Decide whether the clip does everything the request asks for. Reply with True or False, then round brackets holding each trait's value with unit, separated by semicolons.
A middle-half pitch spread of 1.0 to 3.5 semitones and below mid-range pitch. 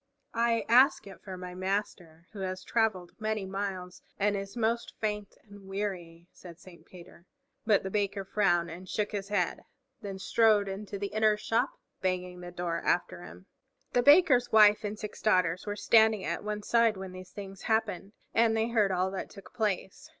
False (2.7 semitones; 200 Hz)